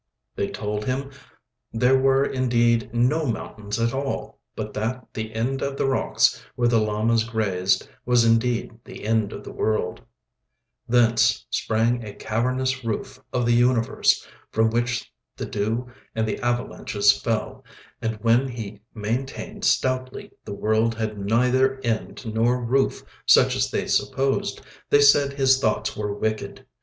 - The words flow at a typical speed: Yes, average, 150 wpm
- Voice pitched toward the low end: Yes, low, 115 Hz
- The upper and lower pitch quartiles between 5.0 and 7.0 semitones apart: No, average, 2.7 semitones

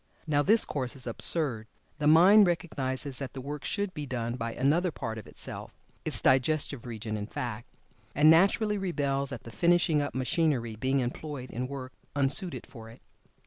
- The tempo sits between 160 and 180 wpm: Yes, average, 175 wpm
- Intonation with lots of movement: No, average, 4.5 semitones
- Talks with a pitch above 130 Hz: Yes, medium, 140 Hz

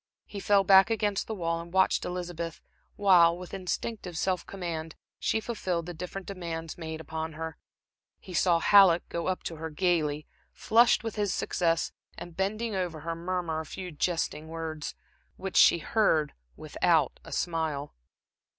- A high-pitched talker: No, medium, 175 Hz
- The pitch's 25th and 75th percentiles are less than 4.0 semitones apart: Yes, average, 2.9 semitones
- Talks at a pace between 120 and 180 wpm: Yes, average, 160 wpm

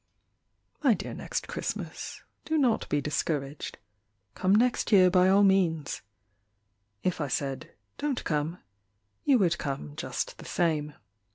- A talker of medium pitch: Yes, medium, 175 Hz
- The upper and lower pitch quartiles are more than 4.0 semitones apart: Yes, wide, 5.5 semitones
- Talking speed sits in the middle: No, slow, 130 wpm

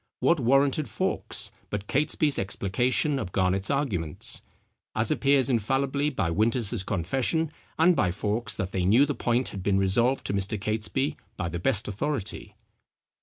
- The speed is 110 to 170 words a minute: Yes, average, 150 wpm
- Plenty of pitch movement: Yes, wide, 6.1 semitones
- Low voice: Yes, low, 115 Hz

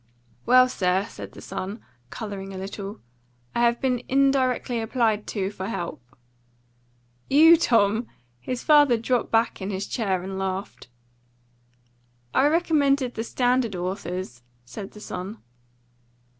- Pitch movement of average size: Yes, average, 4.7 semitones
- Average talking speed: No, slow, 130 wpm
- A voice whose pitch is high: Yes, high, 225 Hz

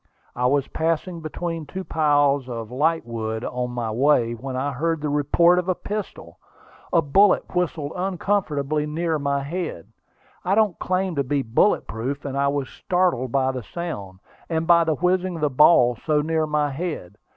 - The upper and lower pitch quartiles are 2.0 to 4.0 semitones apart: No, average, 4.5 semitones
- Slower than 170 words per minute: No, average, 175 wpm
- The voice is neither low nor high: Yes, medium, 150 Hz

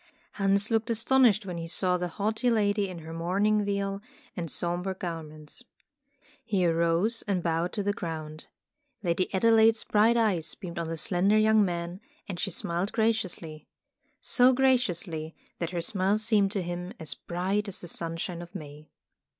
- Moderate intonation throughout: Yes, average, 3.9 semitones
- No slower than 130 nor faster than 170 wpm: Yes, average, 160 wpm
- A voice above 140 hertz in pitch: Yes, medium, 185 Hz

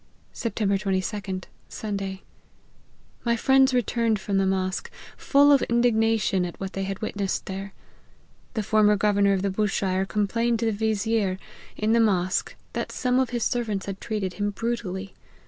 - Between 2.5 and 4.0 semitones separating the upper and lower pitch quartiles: Yes, average, 2.9 semitones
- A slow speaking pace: No, average, 155 wpm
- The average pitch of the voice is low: No, high, 205 Hz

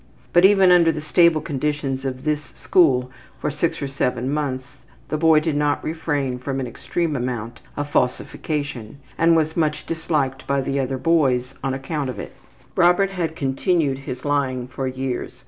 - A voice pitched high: No, medium, 145 Hz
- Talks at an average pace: Yes, average, 170 wpm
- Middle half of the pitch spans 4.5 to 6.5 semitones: No, average, 3.5 semitones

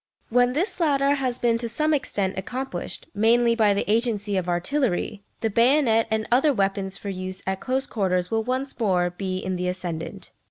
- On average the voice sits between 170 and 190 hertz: No, high, 220 Hz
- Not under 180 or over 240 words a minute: Yes, average, 185 wpm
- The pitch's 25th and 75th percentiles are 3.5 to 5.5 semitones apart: Yes, average, 5.1 semitones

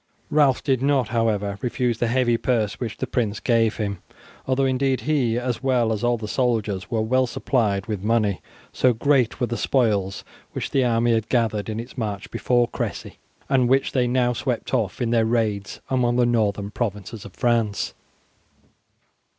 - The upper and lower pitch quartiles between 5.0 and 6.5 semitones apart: No, average, 2.8 semitones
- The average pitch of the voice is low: Yes, low, 120 Hz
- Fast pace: No, average, 175 wpm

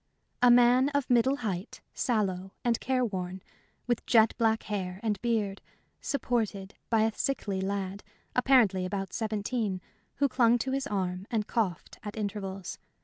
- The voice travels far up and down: No, average, 3.8 semitones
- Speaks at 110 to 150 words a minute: Yes, average, 140 wpm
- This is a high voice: Yes, high, 215 Hz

